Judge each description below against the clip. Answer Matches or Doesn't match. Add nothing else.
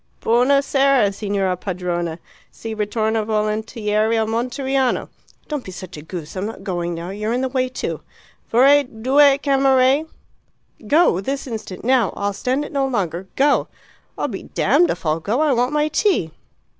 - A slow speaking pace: Doesn't match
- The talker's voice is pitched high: Matches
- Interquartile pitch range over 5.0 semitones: Matches